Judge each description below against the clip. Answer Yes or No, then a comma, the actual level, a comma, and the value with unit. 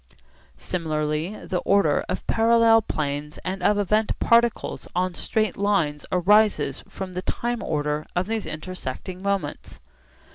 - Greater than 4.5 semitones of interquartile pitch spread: Yes, wide, 5.6 semitones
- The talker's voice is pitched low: No, medium, 185 Hz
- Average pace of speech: No, slow, 130 wpm